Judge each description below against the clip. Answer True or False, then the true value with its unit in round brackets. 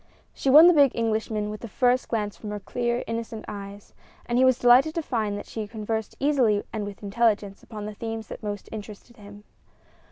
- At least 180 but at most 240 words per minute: True (200 wpm)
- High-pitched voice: True (220 Hz)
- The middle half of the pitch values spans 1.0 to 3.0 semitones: True (2.7 semitones)